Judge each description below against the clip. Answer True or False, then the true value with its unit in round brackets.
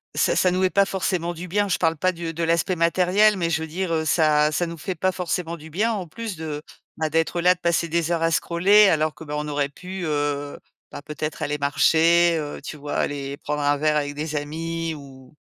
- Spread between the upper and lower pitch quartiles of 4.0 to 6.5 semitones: False (3.0 semitones)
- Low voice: False (165 Hz)